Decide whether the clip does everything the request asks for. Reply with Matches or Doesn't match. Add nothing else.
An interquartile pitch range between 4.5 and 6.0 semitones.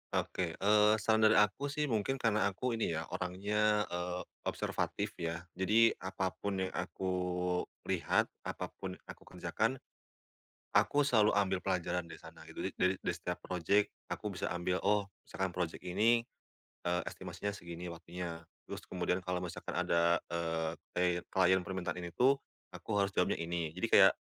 Doesn't match